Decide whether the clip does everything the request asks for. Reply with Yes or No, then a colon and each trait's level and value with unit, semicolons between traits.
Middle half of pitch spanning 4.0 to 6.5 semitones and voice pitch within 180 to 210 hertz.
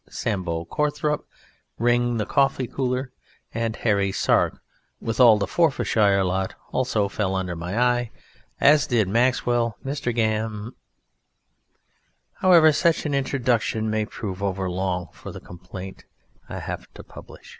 No: average, 4.7 semitones; low, 115 Hz